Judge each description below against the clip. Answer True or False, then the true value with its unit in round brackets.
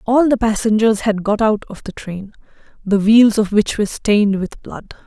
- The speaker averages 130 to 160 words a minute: False (200 wpm)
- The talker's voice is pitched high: True (210 Hz)